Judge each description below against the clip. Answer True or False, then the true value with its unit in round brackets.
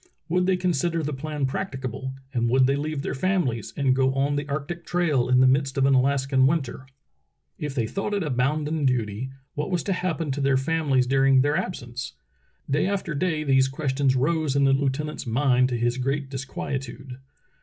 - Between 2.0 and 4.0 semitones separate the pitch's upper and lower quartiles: True (2.8 semitones)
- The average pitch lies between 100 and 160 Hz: True (135 Hz)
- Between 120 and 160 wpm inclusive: False (190 wpm)